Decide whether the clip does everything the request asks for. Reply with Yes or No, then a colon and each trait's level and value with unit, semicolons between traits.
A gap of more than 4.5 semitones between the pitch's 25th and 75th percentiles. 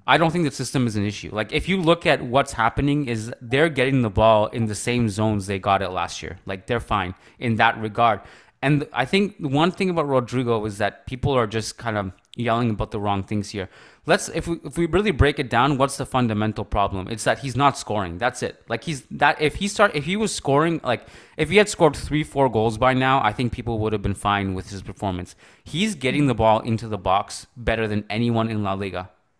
Yes: average, 5.0 semitones